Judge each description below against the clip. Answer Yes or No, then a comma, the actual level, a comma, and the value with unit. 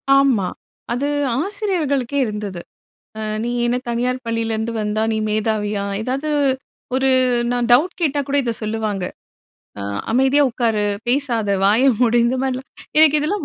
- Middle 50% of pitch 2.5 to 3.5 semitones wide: No, average, 4.1 semitones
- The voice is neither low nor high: No, high, 245 Hz